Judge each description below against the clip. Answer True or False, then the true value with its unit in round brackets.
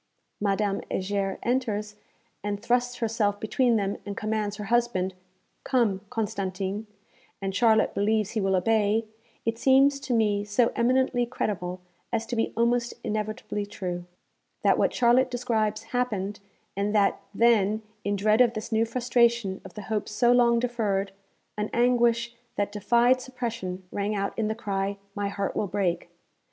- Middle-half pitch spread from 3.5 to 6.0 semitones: False (2.8 semitones)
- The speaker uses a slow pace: False (150 wpm)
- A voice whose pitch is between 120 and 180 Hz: False (215 Hz)